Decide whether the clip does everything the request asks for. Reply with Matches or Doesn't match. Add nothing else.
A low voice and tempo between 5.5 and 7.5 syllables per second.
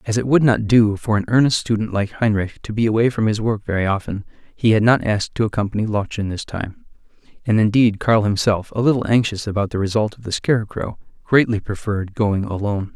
Matches